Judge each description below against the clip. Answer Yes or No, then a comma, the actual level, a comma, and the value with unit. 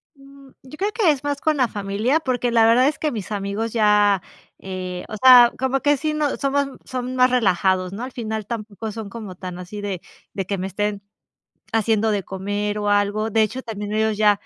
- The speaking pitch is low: No, high, 220 Hz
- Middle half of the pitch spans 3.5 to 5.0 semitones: Yes, average, 4.2 semitones